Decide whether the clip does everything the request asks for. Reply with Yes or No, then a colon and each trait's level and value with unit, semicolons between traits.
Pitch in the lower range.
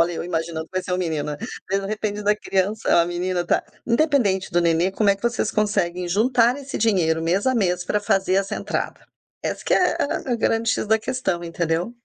No: high, 190 Hz